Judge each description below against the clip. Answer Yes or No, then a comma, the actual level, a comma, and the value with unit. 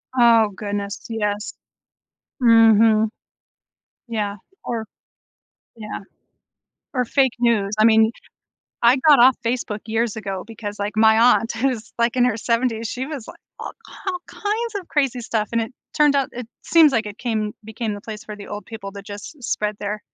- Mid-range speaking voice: No, high, 225 Hz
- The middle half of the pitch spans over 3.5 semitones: No, average, 2.7 semitones